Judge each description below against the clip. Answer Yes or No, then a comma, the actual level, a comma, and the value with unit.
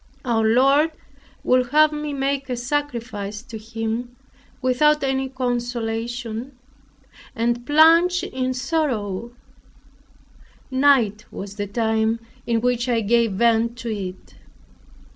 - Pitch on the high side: Yes, high, 240 Hz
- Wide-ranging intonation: No, average, 3.2 semitones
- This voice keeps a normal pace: No, slow, 110 wpm